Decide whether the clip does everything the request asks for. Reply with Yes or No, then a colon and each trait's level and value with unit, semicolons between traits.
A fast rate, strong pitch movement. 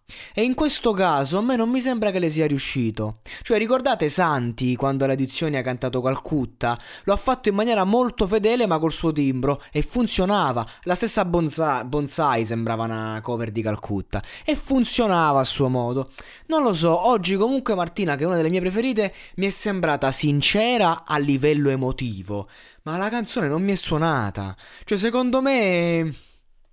Yes: fast, 175 wpm; wide, 8.3 semitones